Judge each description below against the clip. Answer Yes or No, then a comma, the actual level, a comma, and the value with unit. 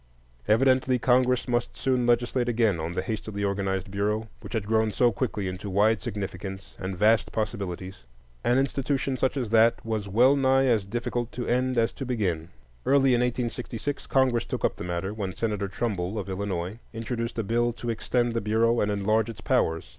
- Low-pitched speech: Yes, low, 115 Hz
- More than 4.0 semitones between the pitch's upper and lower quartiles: No, average, 3.7 semitones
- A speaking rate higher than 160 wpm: Yes, average, 185 wpm